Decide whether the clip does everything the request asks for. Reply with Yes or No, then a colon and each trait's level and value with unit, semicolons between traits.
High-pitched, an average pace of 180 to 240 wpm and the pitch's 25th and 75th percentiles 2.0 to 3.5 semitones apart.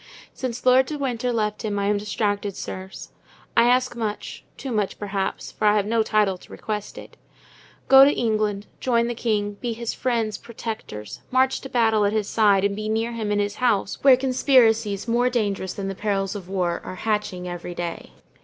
Yes: high, 215 Hz; average, 195 wpm; average, 2.8 semitones